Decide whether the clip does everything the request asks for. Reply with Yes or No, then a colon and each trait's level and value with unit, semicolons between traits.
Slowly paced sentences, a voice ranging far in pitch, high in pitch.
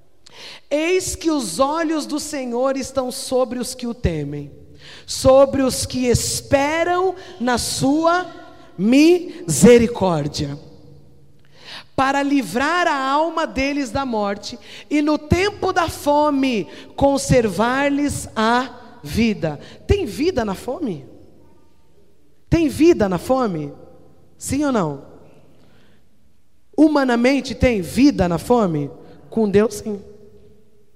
Yes: slow, 105 wpm; wide, 6.0 semitones; very high, 260 Hz